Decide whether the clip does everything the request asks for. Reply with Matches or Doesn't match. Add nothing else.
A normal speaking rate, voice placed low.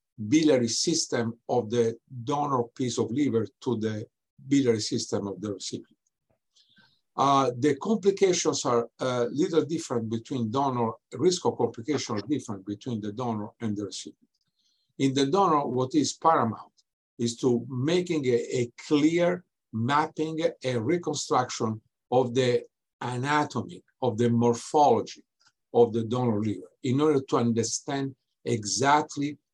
Doesn't match